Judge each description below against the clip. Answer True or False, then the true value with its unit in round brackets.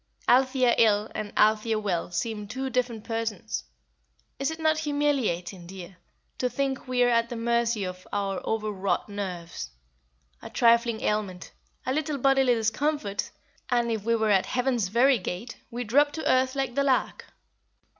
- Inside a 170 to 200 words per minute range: False (160 wpm)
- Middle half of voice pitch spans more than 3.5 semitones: True (4.0 semitones)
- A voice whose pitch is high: True (230 Hz)